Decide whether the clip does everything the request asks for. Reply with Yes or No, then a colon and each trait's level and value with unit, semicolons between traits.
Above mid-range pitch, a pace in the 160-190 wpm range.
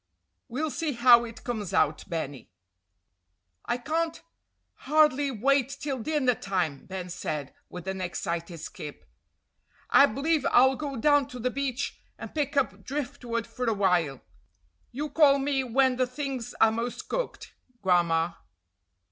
No: high, 245 Hz; average, 140 wpm